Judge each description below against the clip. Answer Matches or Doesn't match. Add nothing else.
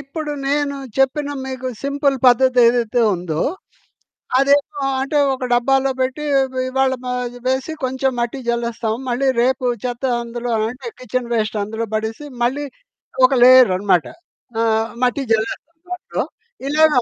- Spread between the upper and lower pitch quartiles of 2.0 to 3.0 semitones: Matches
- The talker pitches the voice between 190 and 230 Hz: Doesn't match